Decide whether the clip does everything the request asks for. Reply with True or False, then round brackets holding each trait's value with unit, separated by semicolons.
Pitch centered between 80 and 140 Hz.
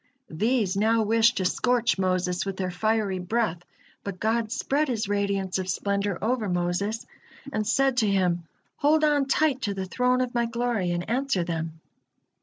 False (210 Hz)